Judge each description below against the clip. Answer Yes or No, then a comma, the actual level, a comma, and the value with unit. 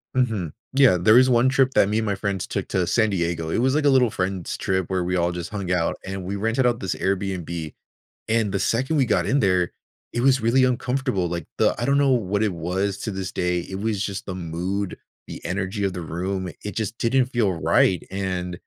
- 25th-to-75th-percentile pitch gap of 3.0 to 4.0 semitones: No, average, 4.5 semitones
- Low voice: Yes, low, 100 Hz